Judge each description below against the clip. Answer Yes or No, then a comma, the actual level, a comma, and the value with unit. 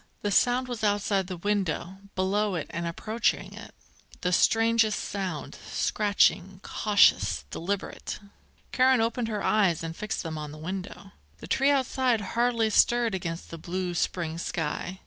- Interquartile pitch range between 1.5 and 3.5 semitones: No, average, 4.3 semitones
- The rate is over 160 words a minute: No, average, 145 wpm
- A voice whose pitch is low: No, high, 200 Hz